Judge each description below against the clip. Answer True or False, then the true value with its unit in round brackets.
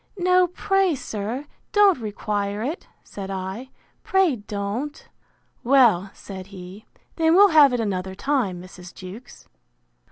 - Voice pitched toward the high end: True (225 Hz)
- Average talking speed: False (125 wpm)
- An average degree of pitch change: False (7.6 semitones)